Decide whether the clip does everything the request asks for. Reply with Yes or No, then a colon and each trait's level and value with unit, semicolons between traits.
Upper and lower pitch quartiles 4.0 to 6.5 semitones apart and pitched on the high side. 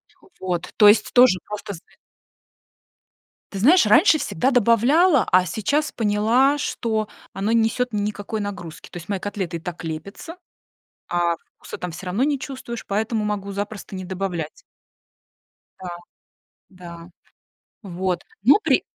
Yes: average, 4.3 semitones; high, 205 Hz